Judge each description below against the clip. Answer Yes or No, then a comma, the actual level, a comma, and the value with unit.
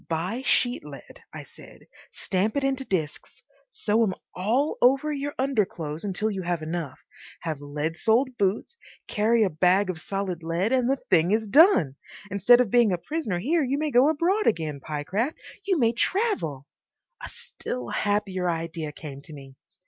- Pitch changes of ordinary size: No, wide, 7.7 semitones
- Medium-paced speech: Yes, average, 170 wpm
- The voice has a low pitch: No, high, 200 Hz